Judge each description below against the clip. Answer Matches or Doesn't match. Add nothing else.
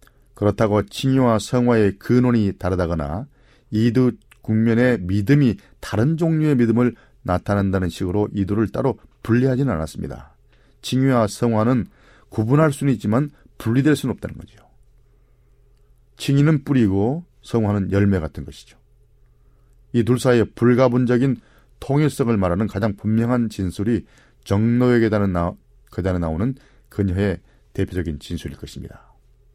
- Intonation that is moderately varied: Matches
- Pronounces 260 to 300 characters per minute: Matches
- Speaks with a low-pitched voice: Matches